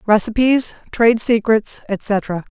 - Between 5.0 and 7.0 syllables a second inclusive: No, 3.8 syllables/s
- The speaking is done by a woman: Yes, female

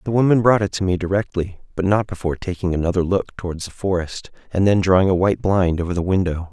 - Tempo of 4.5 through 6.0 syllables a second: No, 6.4 syllables/s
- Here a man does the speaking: Yes, male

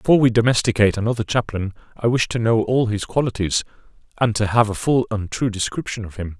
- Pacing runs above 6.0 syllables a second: Yes, 6.3 syllables/s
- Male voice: Yes, male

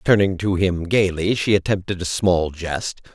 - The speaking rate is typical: Yes, average, 170 wpm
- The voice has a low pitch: Yes, very low, 95 Hz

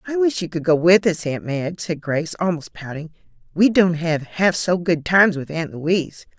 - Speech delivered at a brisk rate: Yes, fast, 215 wpm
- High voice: No, medium, 170 Hz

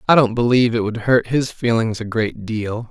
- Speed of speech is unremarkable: No, fast, 225 wpm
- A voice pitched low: Yes, low, 115 Hz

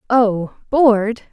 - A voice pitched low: No, high, 225 Hz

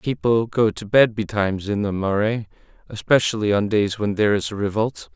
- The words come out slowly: No, average, 185 wpm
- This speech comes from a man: Yes, male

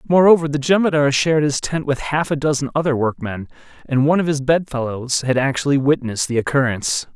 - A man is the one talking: Yes, male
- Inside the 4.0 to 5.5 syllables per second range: No, 6.1 syllables/s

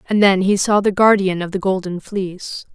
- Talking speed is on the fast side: Yes, fast, 220 wpm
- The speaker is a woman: Yes, female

